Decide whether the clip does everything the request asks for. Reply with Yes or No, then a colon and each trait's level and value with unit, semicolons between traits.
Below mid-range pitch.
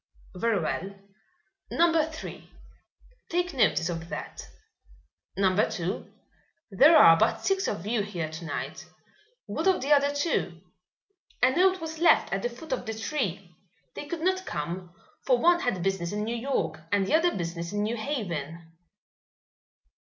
No: high, 215 Hz